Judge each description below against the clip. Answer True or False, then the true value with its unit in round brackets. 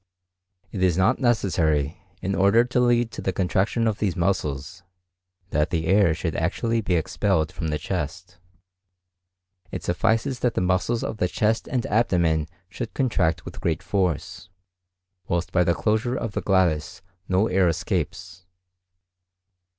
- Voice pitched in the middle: False (95 Hz)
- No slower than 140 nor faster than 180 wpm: True (145 wpm)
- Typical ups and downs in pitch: True (4.4 semitones)